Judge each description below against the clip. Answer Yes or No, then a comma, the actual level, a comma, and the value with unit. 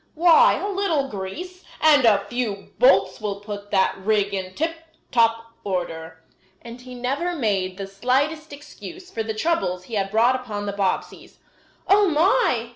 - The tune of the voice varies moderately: No, wide, 7.6 semitones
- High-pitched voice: Yes, high, 230 Hz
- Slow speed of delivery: No, average, 160 wpm